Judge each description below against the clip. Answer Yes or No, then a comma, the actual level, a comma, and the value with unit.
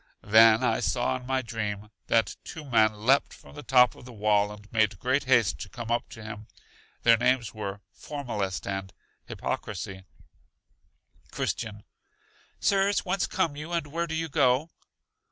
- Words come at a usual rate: Yes, average, 160 wpm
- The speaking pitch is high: No, low, 115 Hz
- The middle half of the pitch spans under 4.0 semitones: No, average, 4.6 semitones